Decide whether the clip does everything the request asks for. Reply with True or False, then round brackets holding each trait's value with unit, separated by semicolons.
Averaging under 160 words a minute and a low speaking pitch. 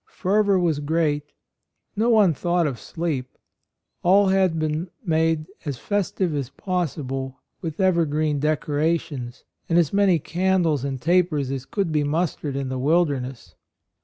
False (140 wpm; 160 Hz)